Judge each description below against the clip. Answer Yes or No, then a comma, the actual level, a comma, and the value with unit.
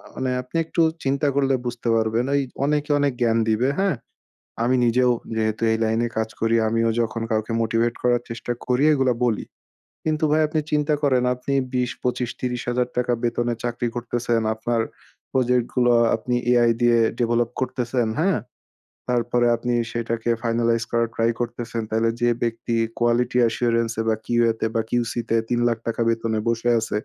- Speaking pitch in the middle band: No, low, 120 Hz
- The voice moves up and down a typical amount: No, narrow, 1.4 semitones